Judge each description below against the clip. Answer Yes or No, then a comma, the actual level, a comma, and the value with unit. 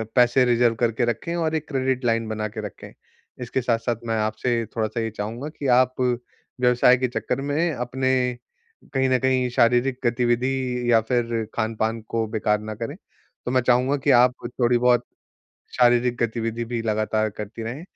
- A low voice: Yes, low, 120 Hz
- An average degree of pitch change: No, narrow, 2.0 semitones